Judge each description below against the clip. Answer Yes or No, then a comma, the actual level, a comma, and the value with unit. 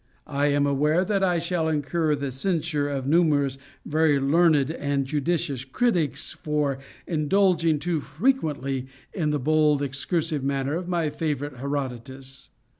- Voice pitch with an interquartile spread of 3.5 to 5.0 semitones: No, average, 3.0 semitones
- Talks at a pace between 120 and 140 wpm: Yes, slow, 135 wpm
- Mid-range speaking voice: Yes, medium, 150 Hz